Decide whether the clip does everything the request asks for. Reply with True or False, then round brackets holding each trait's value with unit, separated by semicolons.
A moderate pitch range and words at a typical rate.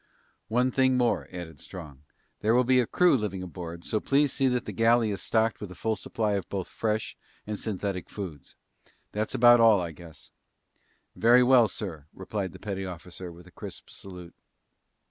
True (4.7 semitones; 185 wpm)